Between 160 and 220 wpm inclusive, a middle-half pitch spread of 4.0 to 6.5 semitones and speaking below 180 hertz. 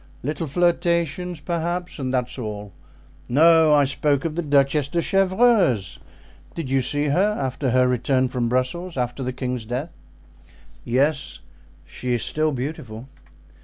No: average, 140 wpm; average, 4.7 semitones; medium, 140 Hz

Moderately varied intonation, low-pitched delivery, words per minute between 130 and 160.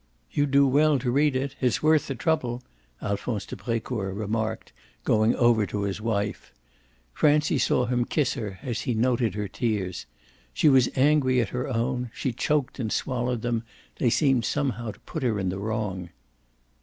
No: average, 3.7 semitones; low, 120 Hz; average, 175 wpm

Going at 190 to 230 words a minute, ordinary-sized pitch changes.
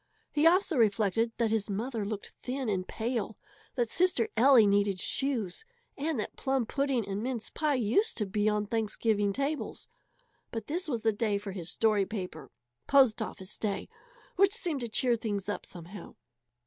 No: average, 170 wpm; average, 4.6 semitones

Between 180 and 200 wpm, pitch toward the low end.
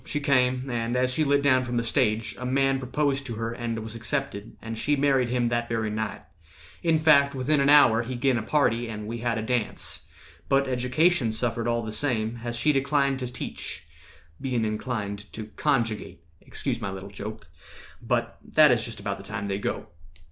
Yes: average, 195 wpm; low, 120 Hz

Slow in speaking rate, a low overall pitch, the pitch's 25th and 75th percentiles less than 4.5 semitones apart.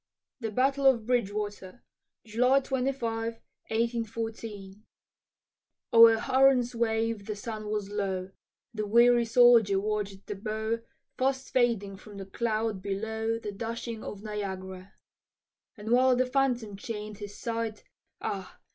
No: slow, 120 wpm; high, 225 Hz; narrow, 2.5 semitones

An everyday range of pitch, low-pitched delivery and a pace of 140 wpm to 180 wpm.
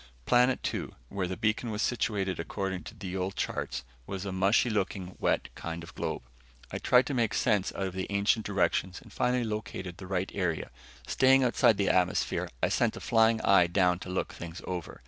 No: average, 3.3 semitones; very low, 95 Hz; average, 200 wpm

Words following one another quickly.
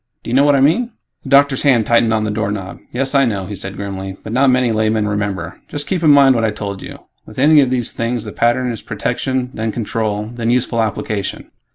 Yes: fast, 235 wpm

